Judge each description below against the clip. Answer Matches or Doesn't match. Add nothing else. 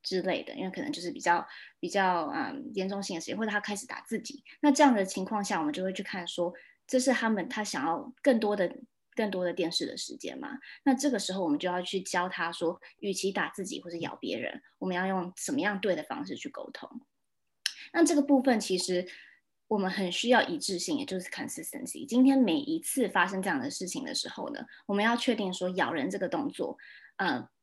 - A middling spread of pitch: Doesn't match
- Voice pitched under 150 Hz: Doesn't match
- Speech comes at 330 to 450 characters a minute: Matches